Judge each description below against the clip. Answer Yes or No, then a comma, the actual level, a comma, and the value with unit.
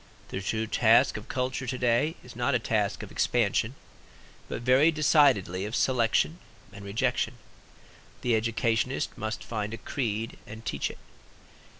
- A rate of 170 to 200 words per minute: No, average, 145 wpm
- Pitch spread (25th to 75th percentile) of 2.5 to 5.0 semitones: Yes, average, 2.8 semitones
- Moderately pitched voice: No, low, 115 Hz